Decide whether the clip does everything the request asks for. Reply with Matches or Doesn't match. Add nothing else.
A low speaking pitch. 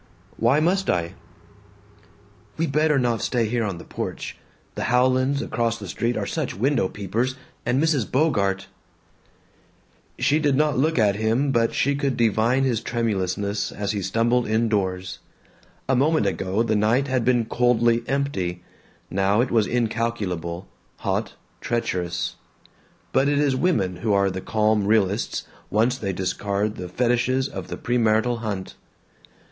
Matches